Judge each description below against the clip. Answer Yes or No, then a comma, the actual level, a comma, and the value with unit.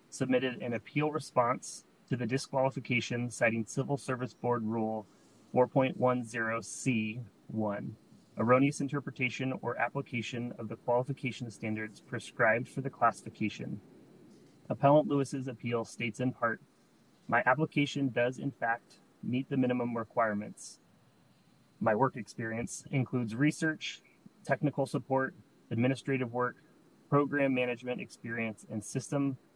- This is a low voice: Yes, low, 125 Hz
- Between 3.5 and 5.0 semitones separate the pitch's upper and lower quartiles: No, average, 2.9 semitones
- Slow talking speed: Yes, slow, 110 wpm